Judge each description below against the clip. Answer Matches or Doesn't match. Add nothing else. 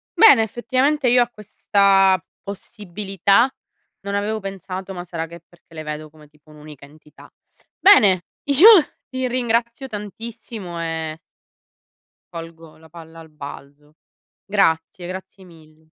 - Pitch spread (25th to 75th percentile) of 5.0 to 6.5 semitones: Matches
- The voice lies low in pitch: Doesn't match